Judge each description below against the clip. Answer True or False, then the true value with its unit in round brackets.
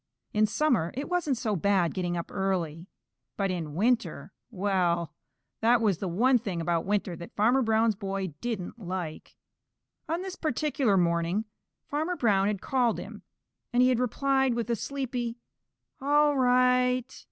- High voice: True (220 Hz)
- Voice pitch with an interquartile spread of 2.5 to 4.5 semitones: False (5.4 semitones)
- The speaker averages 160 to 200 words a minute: False (150 wpm)